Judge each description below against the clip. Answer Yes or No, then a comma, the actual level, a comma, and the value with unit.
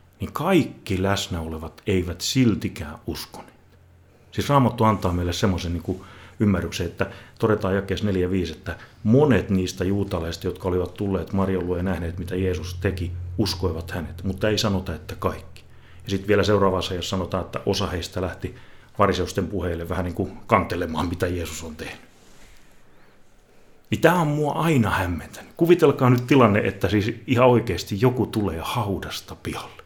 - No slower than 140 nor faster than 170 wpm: Yes, fast, 155 wpm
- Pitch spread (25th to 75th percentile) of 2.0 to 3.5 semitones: Yes, average, 3.0 semitones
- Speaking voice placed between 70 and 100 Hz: Yes, very low, 95 Hz